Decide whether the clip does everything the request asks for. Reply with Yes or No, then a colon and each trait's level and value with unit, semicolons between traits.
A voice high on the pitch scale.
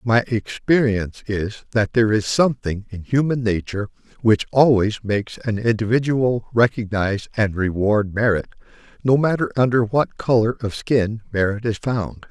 No: low, 110 Hz